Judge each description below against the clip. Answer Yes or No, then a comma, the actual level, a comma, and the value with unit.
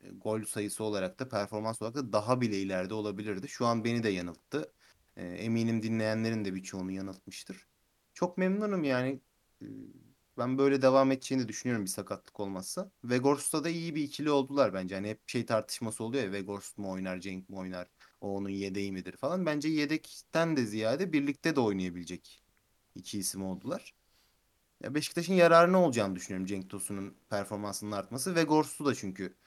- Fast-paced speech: Yes, fast, 165 wpm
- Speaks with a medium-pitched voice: No, low, 110 Hz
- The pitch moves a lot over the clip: Yes, wide, 6.0 semitones